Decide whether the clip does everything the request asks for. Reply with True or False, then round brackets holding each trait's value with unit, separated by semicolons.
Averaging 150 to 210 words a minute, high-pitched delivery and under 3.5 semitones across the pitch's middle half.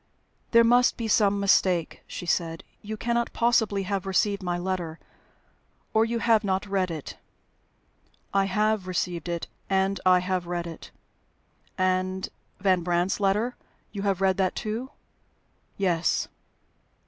False (135 wpm; 195 Hz; 2.8 semitones)